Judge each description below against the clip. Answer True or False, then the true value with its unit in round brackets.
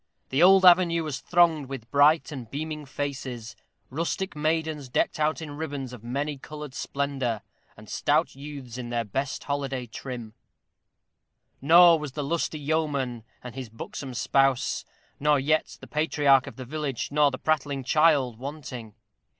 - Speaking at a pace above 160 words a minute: False (150 wpm)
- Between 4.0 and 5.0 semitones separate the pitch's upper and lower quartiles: False (3.1 semitones)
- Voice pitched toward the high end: False (140 Hz)